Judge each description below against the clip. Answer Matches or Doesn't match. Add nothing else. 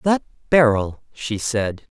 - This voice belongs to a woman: Doesn't match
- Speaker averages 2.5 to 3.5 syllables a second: Matches